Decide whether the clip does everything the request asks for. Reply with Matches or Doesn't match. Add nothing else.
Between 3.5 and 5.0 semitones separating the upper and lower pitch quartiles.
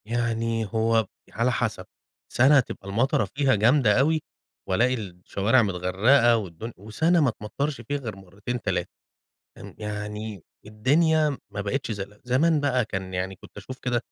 Matches